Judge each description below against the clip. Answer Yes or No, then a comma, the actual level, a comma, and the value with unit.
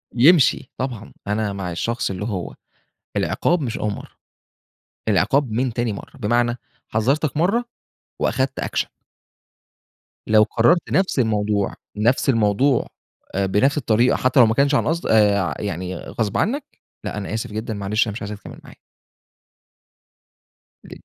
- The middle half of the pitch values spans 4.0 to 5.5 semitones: Yes, average, 4.3 semitones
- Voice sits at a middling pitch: No, low, 115 Hz